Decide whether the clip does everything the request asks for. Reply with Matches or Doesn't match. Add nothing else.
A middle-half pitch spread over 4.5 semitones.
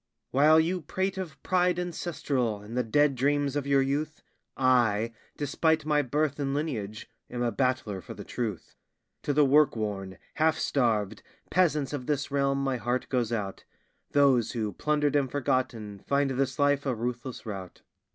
Doesn't match